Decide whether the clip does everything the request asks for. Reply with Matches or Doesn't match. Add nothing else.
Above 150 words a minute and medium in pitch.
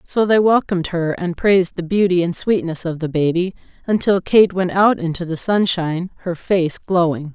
Matches